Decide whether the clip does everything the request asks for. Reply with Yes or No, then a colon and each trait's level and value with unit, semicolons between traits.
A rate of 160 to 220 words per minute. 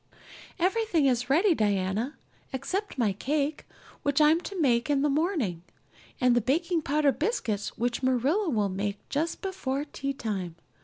No: average, 145 wpm